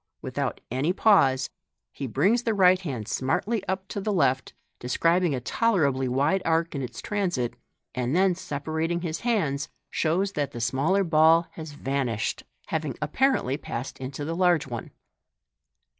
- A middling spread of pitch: No, wide, 5.8 semitones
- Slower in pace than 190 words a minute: Yes, average, 155 wpm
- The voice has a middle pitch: Yes, medium, 160 Hz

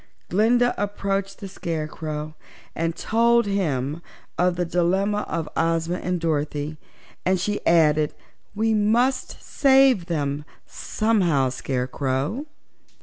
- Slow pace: Yes, slow, 105 wpm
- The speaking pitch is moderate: Yes, medium, 175 Hz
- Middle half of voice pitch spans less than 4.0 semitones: No, wide, 5.4 semitones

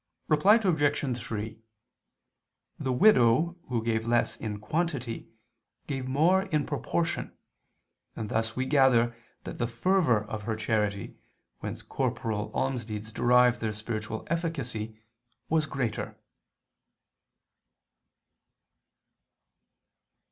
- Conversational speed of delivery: No, slow, 95 wpm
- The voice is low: Yes, low, 120 Hz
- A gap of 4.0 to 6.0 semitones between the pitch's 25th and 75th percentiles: Yes, average, 5.3 semitones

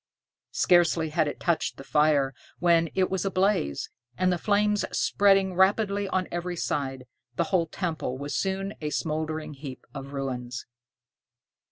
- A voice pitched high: No, medium, 170 Hz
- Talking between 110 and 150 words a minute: Yes, average, 145 wpm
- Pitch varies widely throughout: No, average, 4.6 semitones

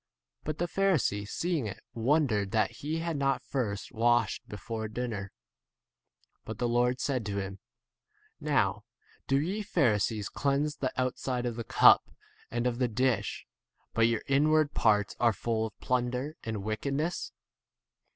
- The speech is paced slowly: No, average, 150 wpm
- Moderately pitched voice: No, low, 120 Hz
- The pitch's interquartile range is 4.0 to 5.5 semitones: Yes, average, 4.3 semitones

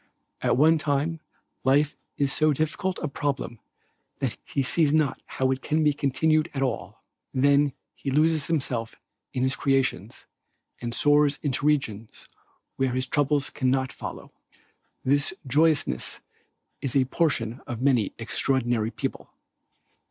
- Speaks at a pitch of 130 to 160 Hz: Yes, medium, 140 Hz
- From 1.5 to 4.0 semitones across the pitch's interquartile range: Yes, narrow, 2.6 semitones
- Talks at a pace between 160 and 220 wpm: No, slow, 135 wpm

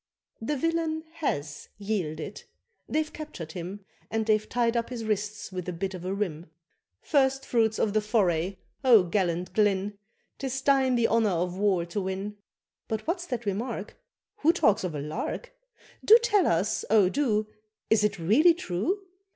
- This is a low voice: No, high, 210 Hz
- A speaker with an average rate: Yes, average, 165 wpm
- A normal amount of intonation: No, wide, 5.7 semitones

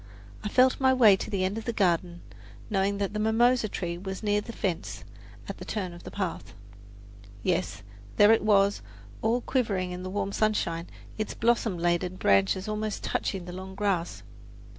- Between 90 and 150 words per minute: No, average, 180 wpm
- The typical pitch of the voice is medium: No, high, 200 Hz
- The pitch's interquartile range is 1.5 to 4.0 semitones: Yes, average, 3.1 semitones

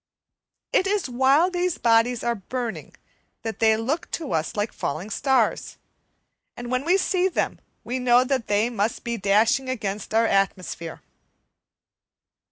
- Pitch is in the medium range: No, high, 240 Hz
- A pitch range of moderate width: Yes, average, 3.6 semitones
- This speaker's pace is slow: No, average, 145 wpm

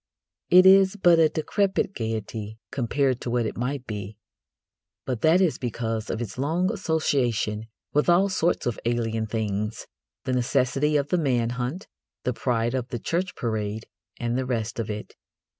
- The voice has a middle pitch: No, low, 125 Hz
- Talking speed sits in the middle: Yes, average, 165 wpm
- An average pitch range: No, wide, 5.8 semitones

